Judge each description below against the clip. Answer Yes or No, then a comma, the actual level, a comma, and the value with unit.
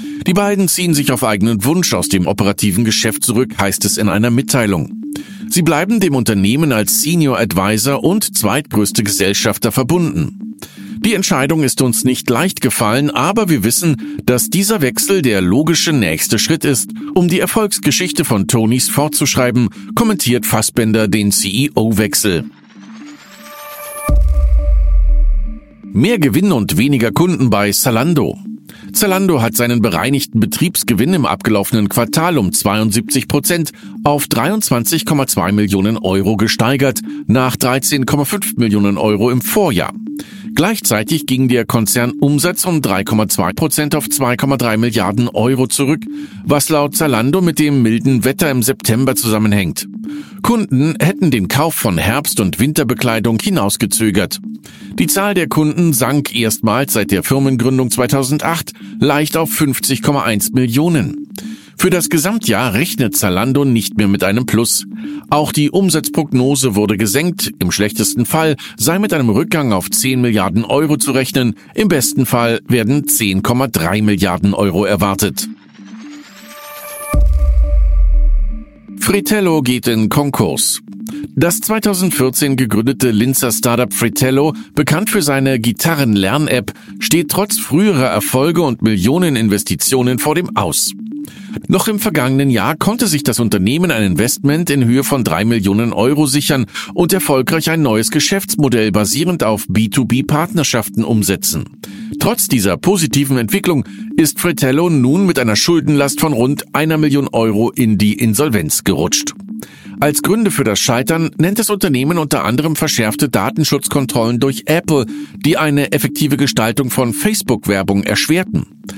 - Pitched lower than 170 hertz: Yes, low, 135 Hz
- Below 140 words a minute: Yes, average, 130 wpm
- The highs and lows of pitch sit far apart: Yes, wide, 6.8 semitones